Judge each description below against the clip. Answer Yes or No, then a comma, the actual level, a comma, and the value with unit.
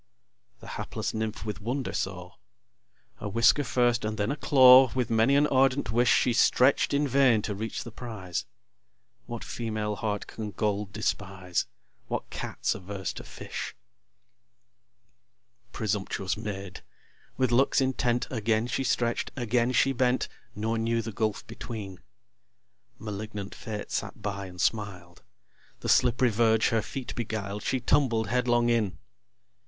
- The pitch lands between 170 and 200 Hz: No, low, 110 Hz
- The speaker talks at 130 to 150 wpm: Yes, average, 140 wpm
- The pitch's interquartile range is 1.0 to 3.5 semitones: Yes, average, 3.1 semitones